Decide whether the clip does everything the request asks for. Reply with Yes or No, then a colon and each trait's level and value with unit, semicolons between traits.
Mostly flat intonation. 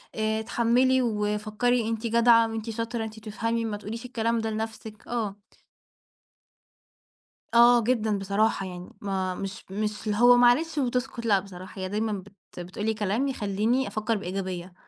Yes: narrow, 2.3 semitones